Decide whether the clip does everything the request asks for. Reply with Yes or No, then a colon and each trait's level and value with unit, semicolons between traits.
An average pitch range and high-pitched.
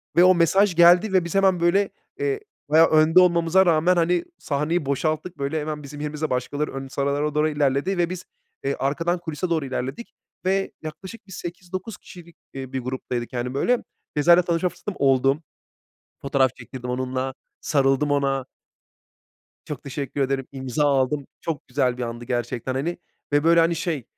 No: average, 4.3 semitones; medium, 150 Hz